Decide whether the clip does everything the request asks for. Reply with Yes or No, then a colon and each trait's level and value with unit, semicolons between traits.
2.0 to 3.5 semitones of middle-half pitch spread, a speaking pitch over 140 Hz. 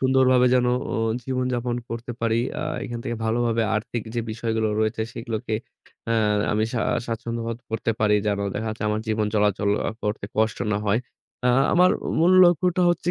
No: narrow, 2.4 semitones; low, 115 Hz